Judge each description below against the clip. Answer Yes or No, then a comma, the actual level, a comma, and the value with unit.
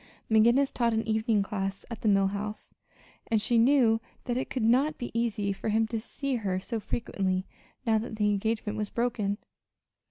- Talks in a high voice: Yes, high, 220 Hz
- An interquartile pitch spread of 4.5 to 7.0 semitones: No, narrow, 2.4 semitones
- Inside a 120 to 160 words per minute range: No, average, 185 wpm